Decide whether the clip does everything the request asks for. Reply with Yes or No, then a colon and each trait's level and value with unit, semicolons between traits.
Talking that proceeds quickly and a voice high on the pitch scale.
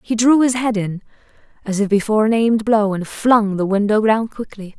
Yes: fast, 215 wpm; high, 215 Hz